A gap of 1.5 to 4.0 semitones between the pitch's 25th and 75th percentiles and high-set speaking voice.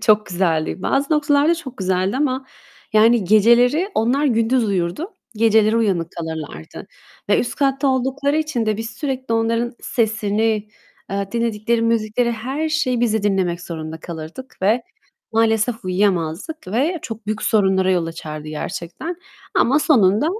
No: wide, 5.4 semitones; high, 225 Hz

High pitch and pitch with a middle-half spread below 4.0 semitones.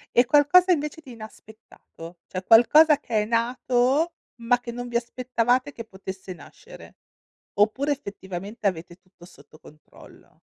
No: high, 235 Hz; average, 4.9 semitones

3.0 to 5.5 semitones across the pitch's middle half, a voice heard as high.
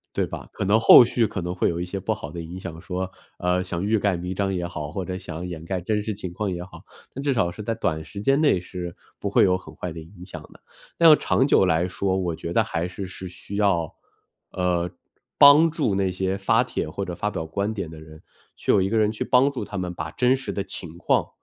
No: average, 3.3 semitones; very low, 95 Hz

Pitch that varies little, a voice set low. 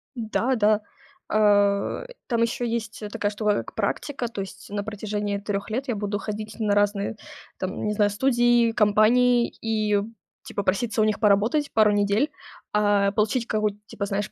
No: narrow, 2.0 semitones; high, 210 Hz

